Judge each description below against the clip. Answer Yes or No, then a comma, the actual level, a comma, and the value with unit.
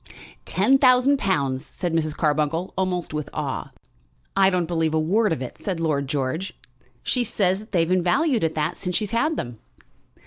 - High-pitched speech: No, medium, 175 Hz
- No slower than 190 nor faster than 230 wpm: No, average, 180 wpm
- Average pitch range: Yes, average, 4.8 semitones